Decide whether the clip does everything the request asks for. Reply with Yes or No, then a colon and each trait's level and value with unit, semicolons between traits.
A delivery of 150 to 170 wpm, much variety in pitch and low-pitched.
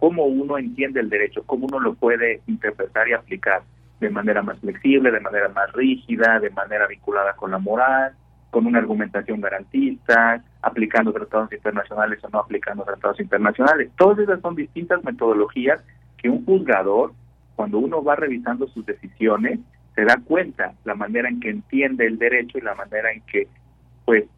Yes: average, 165 wpm; wide, 7.6 semitones; low, 120 Hz